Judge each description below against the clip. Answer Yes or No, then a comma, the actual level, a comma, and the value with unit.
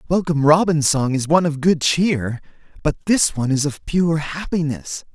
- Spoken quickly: No, average, 175 wpm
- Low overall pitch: No, medium, 155 Hz